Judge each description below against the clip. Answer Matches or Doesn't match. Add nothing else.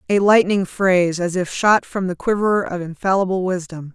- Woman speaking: Matches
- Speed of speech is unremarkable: Matches